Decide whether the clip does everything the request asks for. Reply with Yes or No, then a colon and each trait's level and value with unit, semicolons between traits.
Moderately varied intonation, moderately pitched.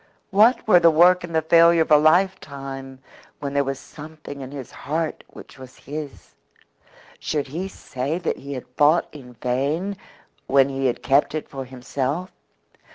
Yes: average, 3.7 semitones; medium, 145 Hz